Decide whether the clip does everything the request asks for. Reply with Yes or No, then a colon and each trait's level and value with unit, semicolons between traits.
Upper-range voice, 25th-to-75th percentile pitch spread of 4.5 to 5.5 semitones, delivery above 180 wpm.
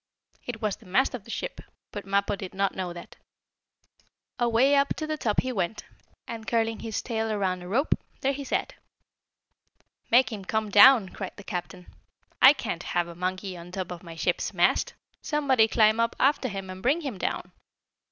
Yes: high, 215 Hz; average, 5.0 semitones; average, 190 wpm